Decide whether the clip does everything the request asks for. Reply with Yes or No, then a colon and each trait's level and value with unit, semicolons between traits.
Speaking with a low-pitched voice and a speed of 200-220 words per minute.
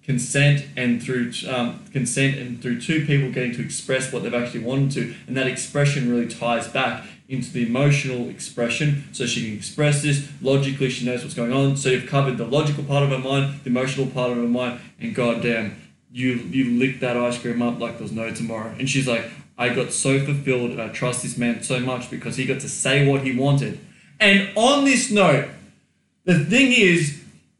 Yes: low, 130 Hz; fast, 205 wpm